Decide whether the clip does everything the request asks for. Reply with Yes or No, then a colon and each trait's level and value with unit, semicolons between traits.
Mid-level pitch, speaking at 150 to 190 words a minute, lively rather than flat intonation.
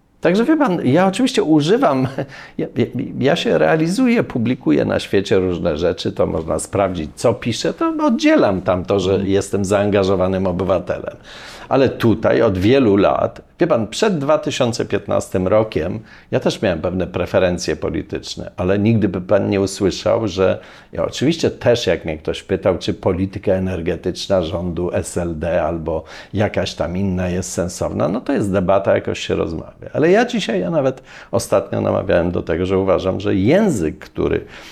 No: low, 100 Hz; average, 155 wpm; wide, 6.6 semitones